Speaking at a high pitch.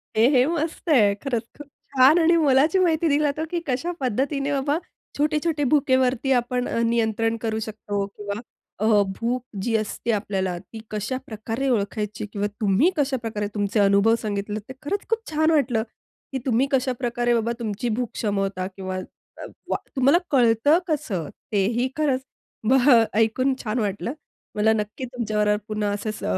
Yes: high, 235 Hz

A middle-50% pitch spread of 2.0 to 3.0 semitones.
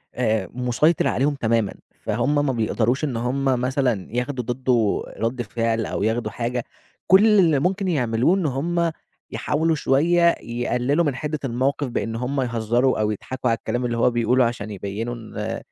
No: average, 3.8 semitones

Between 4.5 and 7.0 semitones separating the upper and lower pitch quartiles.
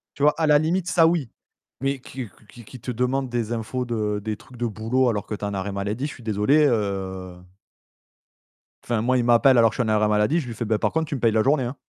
No: average, 4.1 semitones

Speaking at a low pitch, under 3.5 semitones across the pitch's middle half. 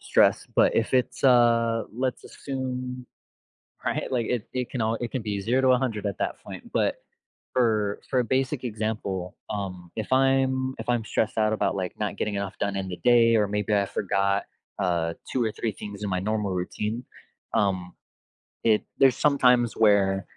No: low, 110 Hz; average, 3.9 semitones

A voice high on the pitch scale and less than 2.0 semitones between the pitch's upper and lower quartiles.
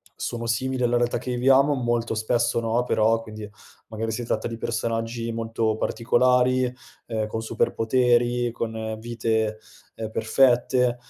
No: low, 115 Hz; narrow, 1.6 semitones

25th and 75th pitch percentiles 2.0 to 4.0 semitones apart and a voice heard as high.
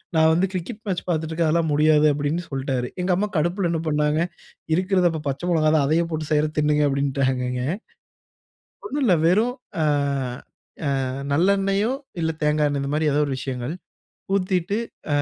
No: average, 3.4 semitones; medium, 155 Hz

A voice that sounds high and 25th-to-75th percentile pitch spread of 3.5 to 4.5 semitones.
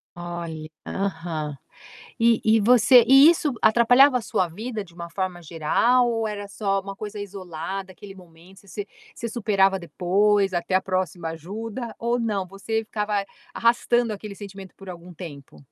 Yes: high, 195 Hz; average, 4.0 semitones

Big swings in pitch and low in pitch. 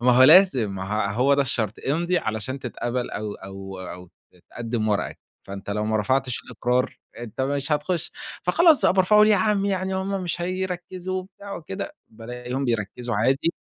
Yes: wide, 8.9 semitones; low, 130 Hz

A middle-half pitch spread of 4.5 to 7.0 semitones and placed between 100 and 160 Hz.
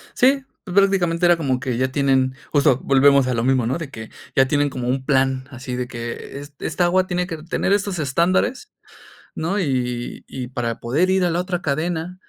Yes: wide, 5.4 semitones; medium, 140 Hz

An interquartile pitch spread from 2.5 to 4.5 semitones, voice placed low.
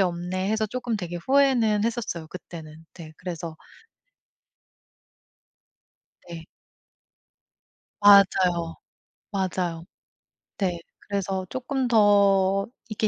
No: average, 3.8 semitones; high, 190 Hz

